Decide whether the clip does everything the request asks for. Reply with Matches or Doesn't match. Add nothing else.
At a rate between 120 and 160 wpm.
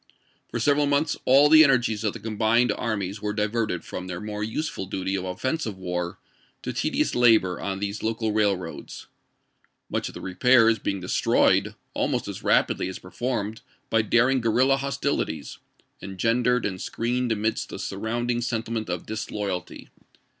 Matches